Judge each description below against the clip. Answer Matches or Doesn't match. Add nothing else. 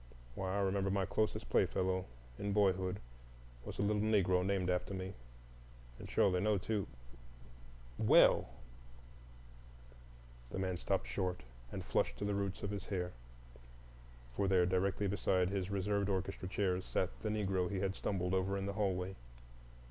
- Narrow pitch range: Matches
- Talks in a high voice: Doesn't match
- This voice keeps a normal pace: Matches